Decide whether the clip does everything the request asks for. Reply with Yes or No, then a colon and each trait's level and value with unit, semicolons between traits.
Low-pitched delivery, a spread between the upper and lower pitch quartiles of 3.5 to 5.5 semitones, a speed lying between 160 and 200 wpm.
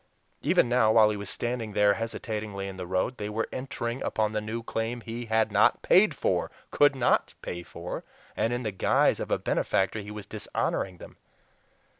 No: low, 110 Hz; narrow, 2.4 semitones; average, 190 wpm